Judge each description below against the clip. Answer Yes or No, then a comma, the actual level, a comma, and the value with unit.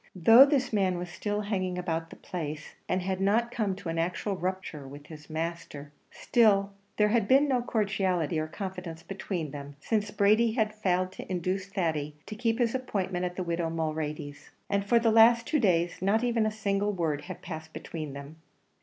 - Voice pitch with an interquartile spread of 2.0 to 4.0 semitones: No, average, 4.6 semitones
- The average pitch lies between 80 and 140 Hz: No, medium, 185 Hz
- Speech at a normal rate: Yes, average, 190 wpm